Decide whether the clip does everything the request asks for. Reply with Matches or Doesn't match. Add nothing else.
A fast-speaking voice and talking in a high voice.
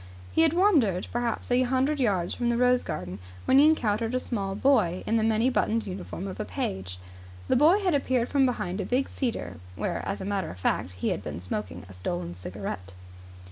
Matches